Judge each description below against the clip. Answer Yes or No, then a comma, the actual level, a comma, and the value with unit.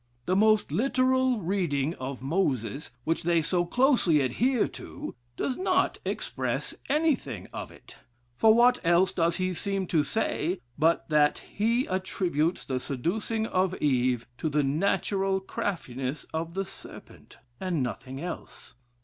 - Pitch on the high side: No, medium, 180 Hz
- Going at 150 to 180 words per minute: No, average, 140 wpm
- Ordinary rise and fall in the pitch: No, wide, 6.3 semitones